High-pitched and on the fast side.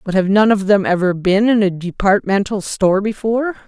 No: high, 200 Hz; average, 195 wpm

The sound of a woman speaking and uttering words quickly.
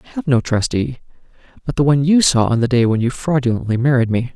No: male; fast, 235 wpm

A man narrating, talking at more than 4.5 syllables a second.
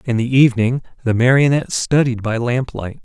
Yes: male; 5.5 syllables/s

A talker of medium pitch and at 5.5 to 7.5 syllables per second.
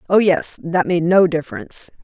No: medium, 180 Hz; 5.2 syllables/s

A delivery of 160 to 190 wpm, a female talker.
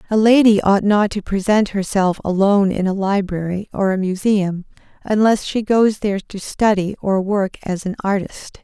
Yes: average, 175 wpm; female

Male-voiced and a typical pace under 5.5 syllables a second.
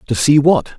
Yes: male; 5.3 syllables/s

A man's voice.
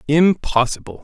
Yes: male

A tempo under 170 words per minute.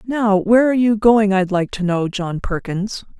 No: fast, 205 wpm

